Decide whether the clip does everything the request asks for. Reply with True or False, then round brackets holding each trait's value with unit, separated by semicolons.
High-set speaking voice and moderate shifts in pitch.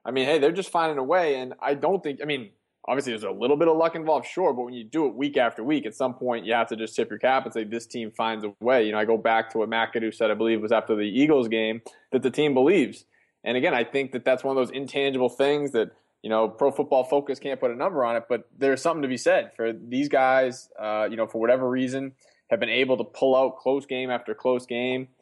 False (130 Hz; 3.3 semitones)